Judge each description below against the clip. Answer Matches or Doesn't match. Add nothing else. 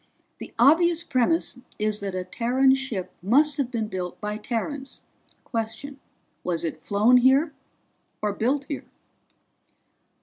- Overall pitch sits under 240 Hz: Doesn't match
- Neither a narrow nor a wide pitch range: Matches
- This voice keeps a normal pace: Doesn't match